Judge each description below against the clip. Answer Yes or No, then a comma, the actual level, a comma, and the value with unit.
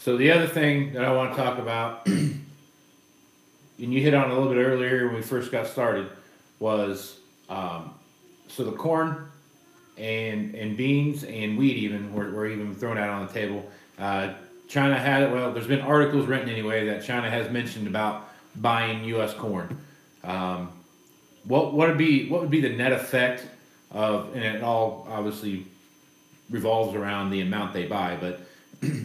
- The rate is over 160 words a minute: Yes, average, 175 wpm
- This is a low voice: Yes, low, 115 Hz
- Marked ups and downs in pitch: No, average, 4.4 semitones